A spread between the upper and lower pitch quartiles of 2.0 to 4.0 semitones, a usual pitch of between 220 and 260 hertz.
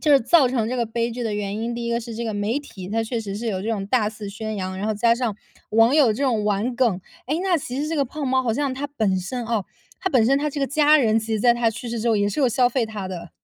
Yes: average, 3.5 semitones; high, 230 Hz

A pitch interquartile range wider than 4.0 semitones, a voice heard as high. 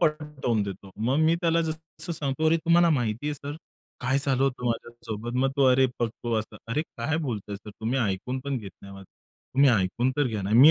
No: average, 5.2 semitones; low, 130 Hz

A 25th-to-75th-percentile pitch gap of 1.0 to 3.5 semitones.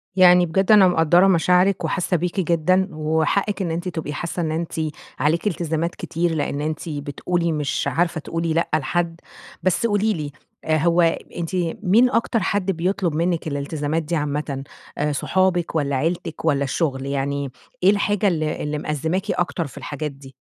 Yes: average, 3.1 semitones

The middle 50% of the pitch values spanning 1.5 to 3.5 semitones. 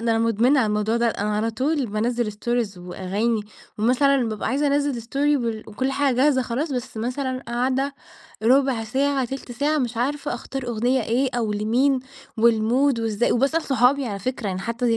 Yes: average, 3.2 semitones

